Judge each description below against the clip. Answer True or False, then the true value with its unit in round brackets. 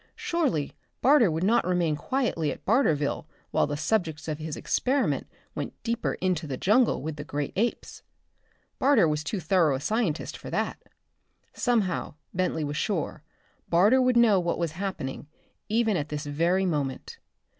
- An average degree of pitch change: False (6.6 semitones)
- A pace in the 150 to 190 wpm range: True (155 wpm)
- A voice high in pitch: False (175 Hz)